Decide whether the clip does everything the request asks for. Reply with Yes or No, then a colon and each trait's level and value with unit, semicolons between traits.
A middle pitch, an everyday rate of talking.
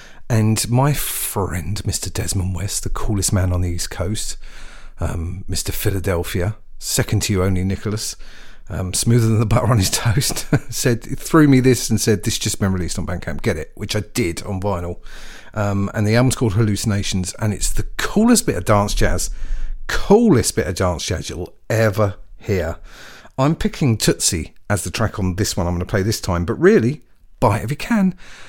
No: low, 105 Hz; average, 190 wpm